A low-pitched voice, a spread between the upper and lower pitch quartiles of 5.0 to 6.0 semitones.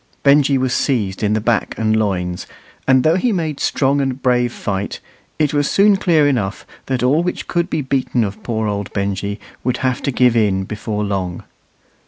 Yes: low, 125 Hz; average, 5.3 semitones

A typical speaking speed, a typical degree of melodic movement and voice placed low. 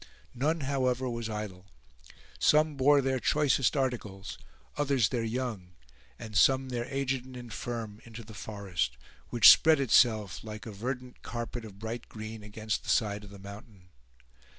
Yes: average, 150 wpm; average, 3.7 semitones; low, 115 Hz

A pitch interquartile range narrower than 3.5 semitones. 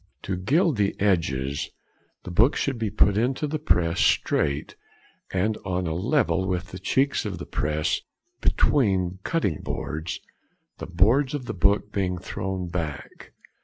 No: average, 4.8 semitones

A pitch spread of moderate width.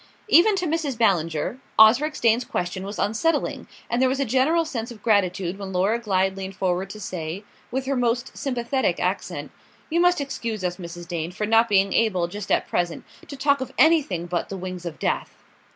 No: wide, 6.1 semitones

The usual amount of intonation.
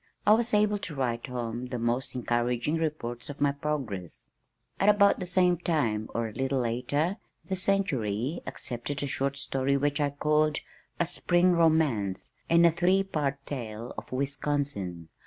No: wide, 5.7 semitones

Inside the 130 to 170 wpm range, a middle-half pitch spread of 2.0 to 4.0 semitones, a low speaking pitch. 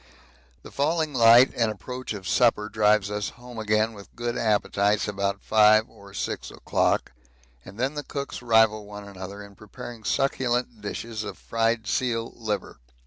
Yes: average, 155 wpm; narrow, 2.6 semitones; low, 110 Hz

